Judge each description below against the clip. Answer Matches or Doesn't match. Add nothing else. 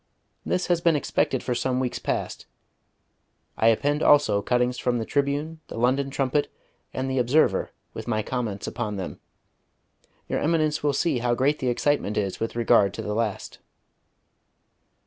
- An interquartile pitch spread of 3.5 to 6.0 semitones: Matches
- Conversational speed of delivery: Matches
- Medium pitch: Doesn't match